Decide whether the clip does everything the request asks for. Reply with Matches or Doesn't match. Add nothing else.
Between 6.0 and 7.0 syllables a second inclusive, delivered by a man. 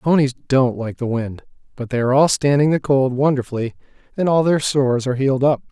Matches